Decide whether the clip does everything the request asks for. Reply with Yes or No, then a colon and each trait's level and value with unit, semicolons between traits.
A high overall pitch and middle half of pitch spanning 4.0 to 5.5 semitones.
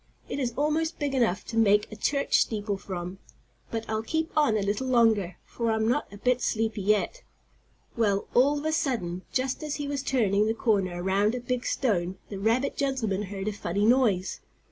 Yes: high, 225 Hz; average, 4.7 semitones